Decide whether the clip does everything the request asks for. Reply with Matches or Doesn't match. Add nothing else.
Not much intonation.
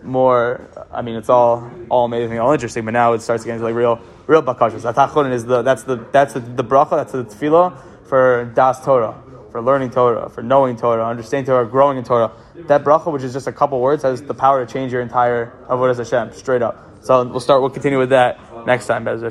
Matches